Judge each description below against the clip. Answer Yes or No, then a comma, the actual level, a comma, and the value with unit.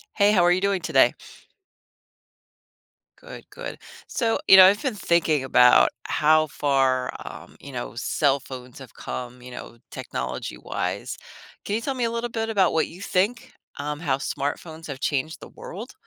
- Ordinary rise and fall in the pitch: No, wide, 7.2 semitones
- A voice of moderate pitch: Yes, medium, 155 Hz